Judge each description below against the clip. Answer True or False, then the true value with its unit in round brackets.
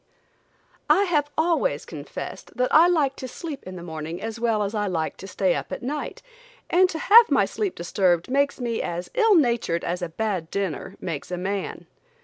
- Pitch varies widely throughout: True (9.0 semitones)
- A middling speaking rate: True (195 wpm)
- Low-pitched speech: False (225 Hz)